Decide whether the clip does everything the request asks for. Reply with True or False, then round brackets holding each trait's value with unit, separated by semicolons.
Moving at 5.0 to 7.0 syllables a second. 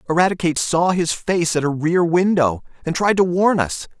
True (5.2 syllables/s)